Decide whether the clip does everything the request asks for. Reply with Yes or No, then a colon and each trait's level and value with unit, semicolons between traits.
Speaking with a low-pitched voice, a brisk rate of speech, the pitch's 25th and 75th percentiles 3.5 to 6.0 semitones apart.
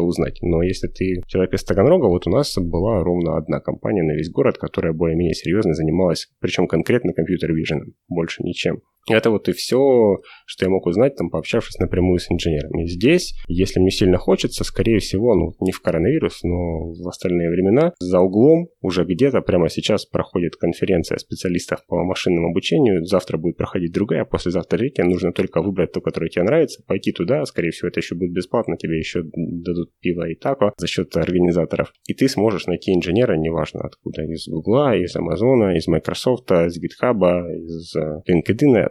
No: very low, 90 Hz; fast, 175 wpm; narrow, 2.4 semitones